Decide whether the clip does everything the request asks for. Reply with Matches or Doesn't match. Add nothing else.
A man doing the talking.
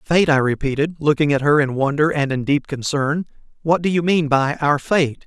Matches